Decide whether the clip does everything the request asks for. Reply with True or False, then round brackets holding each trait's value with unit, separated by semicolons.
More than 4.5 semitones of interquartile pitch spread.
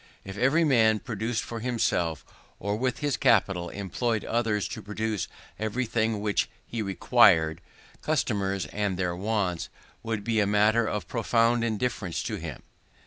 False (3.1 semitones)